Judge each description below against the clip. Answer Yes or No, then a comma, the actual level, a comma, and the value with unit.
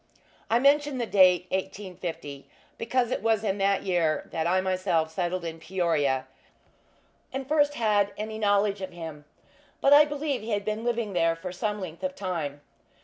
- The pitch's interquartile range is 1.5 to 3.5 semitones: No, average, 4.8 semitones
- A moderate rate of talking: Yes, average, 175 wpm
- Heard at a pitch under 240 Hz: Yes, high, 190 Hz